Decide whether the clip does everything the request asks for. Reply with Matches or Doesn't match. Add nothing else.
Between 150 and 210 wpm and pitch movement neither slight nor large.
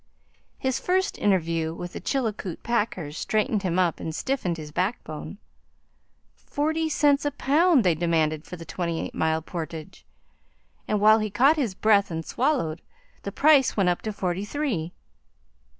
Doesn't match